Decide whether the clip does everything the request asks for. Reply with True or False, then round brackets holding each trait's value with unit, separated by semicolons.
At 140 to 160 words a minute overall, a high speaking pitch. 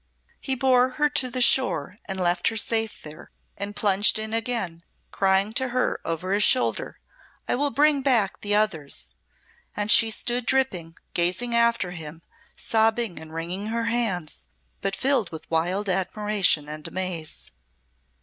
True (150 wpm; 205 Hz)